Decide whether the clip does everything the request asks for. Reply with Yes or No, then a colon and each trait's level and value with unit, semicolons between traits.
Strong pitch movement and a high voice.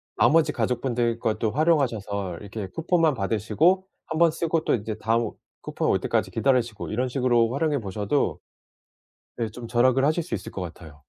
No: wide, 5.8 semitones; low, 120 Hz